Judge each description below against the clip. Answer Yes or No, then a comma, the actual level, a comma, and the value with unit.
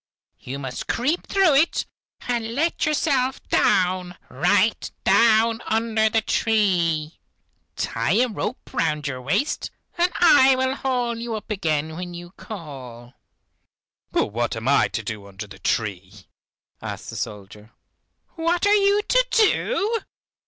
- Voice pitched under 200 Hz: No, high, 215 Hz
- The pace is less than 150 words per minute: Yes, average, 140 wpm